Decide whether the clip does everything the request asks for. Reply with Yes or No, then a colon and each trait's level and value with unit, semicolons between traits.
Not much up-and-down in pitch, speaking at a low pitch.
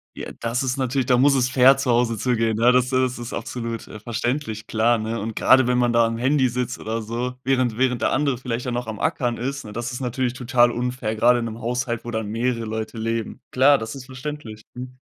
Yes: narrow, 1.9 semitones; low, 120 Hz